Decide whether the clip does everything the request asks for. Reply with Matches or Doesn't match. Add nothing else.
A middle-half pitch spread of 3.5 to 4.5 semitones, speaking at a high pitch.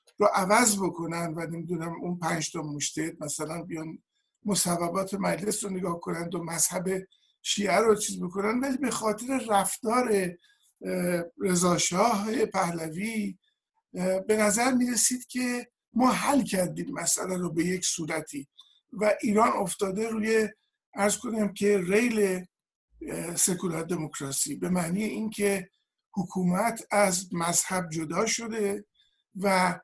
Matches